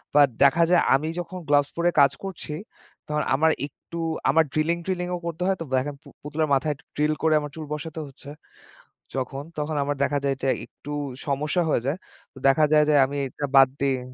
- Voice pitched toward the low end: No, medium, 150 Hz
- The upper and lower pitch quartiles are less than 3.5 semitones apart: Yes, narrow, 2.5 semitones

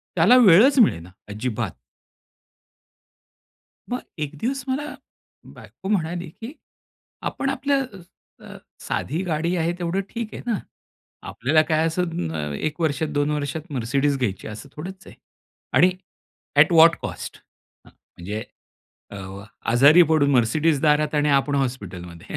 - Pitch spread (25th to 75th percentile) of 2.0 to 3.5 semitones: No, average, 5.2 semitones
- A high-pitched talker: No, medium, 155 Hz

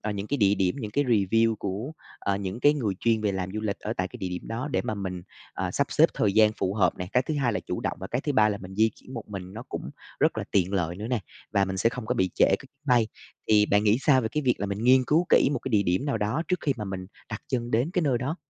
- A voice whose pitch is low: Yes, low, 110 Hz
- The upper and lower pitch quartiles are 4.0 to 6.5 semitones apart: Yes, average, 4.5 semitones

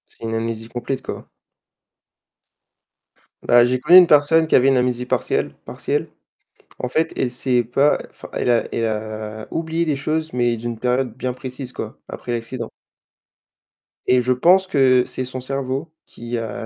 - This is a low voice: Yes, low, 125 Hz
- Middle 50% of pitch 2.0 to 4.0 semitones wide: Yes, narrow, 2.6 semitones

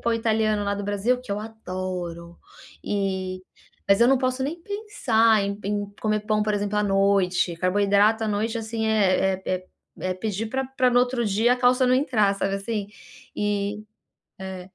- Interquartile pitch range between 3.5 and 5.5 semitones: No, average, 2.7 semitones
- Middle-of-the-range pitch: No, high, 210 Hz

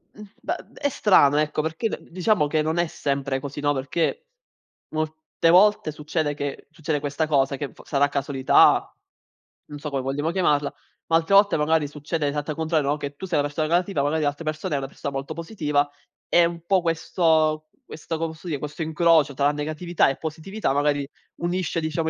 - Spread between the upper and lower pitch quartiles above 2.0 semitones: Yes, narrow, 2.4 semitones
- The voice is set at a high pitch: No, medium, 155 Hz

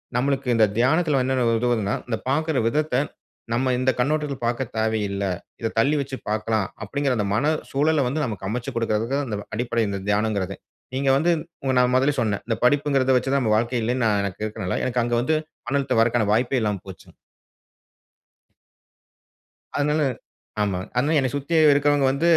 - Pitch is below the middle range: Yes, low, 125 Hz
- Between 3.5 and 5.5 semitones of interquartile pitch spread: Yes, average, 4.1 semitones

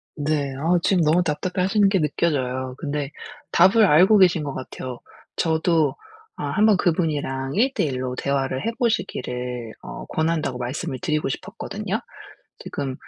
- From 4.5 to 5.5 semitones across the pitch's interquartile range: Yes, average, 5.2 semitones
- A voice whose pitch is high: No, medium, 150 Hz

